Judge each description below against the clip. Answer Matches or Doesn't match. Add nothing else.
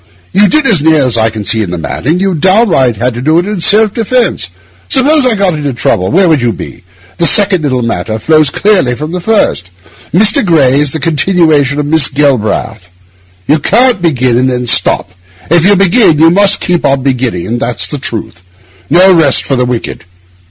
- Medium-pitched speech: Matches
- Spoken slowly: Doesn't match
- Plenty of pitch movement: Matches